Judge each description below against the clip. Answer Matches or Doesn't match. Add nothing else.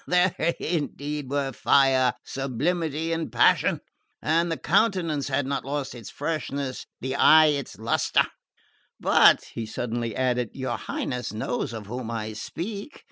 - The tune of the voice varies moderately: Matches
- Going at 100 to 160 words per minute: Matches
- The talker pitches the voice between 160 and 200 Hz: Doesn't match